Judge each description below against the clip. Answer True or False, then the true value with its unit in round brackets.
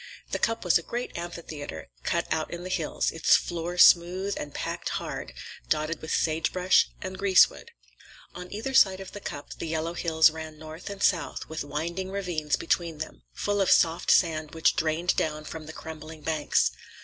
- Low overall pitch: False (165 Hz)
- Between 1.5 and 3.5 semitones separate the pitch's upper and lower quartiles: True (2.7 semitones)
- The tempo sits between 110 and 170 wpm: False (180 wpm)